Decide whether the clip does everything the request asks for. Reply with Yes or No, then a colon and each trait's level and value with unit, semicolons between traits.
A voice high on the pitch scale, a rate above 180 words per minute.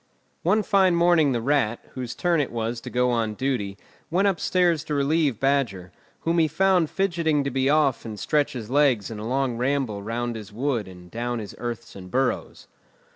No: low, 135 Hz; average, 190 wpm